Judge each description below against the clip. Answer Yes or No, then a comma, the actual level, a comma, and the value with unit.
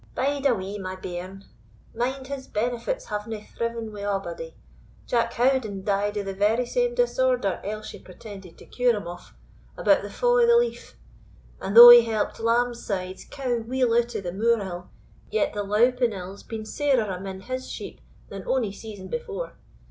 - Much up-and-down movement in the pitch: No, average, 4.3 semitones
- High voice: Yes, high, 225 Hz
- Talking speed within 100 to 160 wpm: No, average, 170 wpm